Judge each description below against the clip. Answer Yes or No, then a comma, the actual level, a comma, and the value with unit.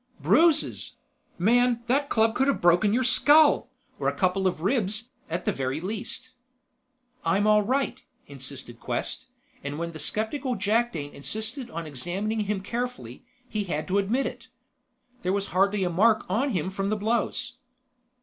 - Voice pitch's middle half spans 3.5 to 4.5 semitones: No, wide, 5.4 semitones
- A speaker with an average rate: Yes, average, 160 wpm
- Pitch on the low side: No, high, 210 Hz